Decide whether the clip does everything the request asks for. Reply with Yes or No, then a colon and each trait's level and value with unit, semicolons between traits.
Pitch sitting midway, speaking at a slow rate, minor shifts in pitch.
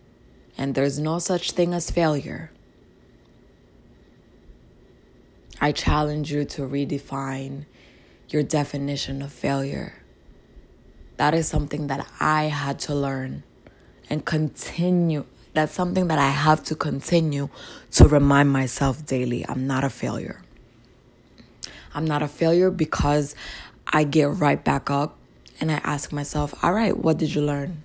Yes: medium, 145 Hz; slow, 130 wpm; narrow, 2.2 semitones